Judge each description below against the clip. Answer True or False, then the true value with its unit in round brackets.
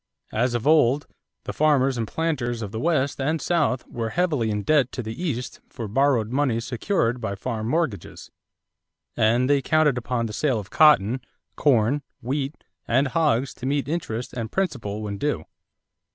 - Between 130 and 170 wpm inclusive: True (165 wpm)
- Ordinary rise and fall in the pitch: True (4.5 semitones)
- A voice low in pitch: True (130 Hz)